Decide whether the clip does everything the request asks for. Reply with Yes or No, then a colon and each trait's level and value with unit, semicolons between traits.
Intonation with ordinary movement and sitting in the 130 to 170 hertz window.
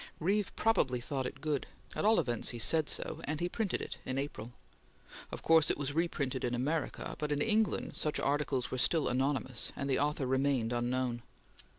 Yes: average, 3.5 semitones; medium, 140 Hz